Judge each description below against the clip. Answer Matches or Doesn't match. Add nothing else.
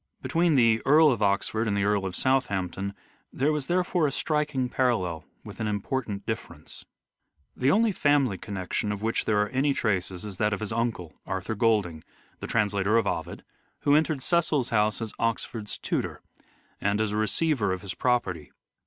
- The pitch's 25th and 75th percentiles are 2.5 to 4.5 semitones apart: Doesn't match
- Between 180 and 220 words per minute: Matches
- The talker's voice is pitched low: Matches